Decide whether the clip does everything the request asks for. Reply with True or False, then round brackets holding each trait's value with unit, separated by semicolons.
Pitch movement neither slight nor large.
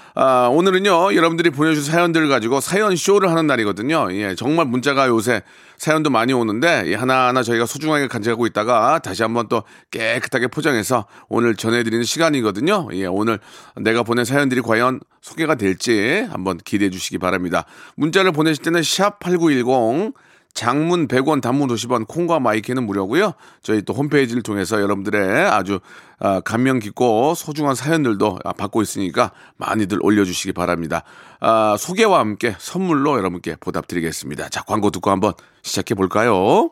False (6.8 semitones)